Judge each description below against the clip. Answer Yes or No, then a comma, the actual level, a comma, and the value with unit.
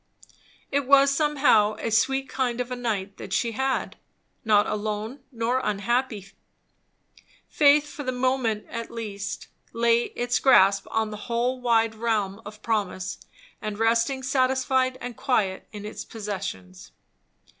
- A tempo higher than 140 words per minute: No, slow, 135 wpm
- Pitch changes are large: No, average, 3.5 semitones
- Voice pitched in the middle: No, high, 230 Hz